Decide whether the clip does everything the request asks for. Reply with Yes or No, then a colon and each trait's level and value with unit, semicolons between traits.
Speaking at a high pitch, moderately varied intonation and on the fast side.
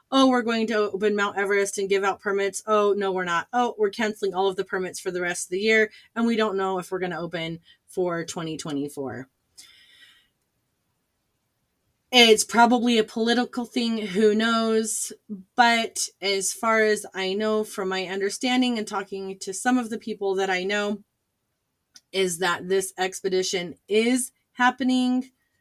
No: high, 205 Hz; average, 3.0 semitones; average, 165 wpm